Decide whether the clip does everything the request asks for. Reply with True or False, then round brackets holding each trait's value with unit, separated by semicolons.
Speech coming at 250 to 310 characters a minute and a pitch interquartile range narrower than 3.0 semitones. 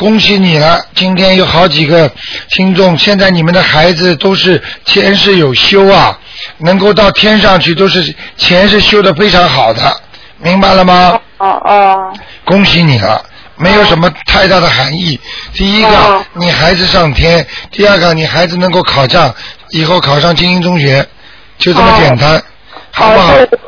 False (240 characters per minute; 2.5 semitones)